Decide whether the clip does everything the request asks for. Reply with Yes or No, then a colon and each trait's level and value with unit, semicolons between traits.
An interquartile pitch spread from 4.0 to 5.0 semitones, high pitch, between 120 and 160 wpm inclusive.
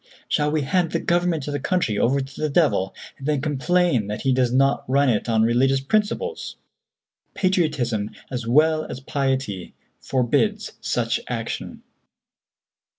No: average, 4.5 semitones; low, 135 Hz; average, 150 wpm